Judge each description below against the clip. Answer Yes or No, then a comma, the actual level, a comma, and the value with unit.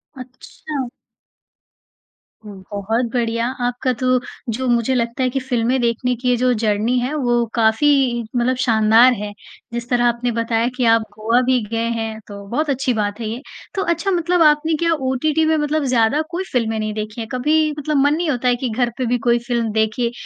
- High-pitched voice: Yes, high, 245 Hz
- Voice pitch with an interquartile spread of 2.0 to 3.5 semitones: Yes, average, 2.8 semitones